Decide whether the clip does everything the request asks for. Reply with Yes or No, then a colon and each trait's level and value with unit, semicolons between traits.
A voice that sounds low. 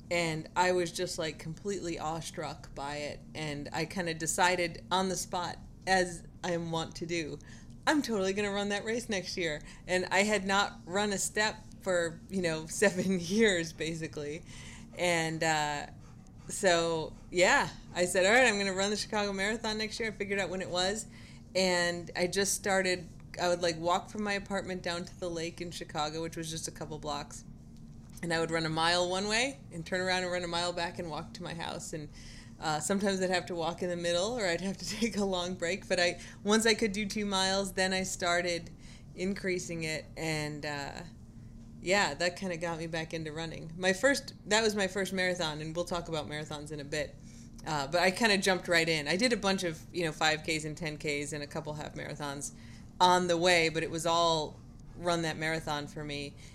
No: medium, 175 Hz